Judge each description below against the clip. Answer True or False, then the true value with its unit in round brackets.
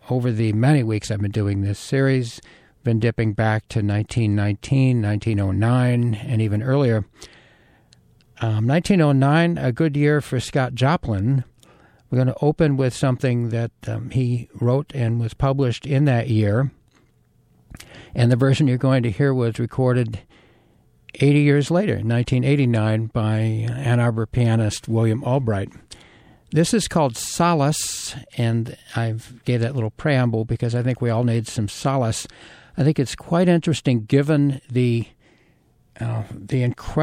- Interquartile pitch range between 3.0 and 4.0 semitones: True (3.4 semitones)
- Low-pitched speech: True (120 Hz)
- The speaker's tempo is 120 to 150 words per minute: True (145 wpm)